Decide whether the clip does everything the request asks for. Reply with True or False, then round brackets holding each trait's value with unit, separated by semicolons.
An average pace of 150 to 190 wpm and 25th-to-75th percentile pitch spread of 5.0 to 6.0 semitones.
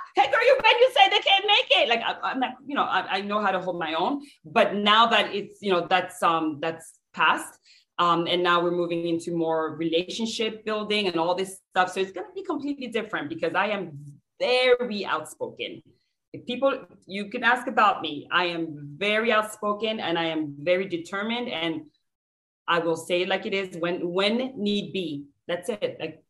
False (205 wpm; 5.4 semitones)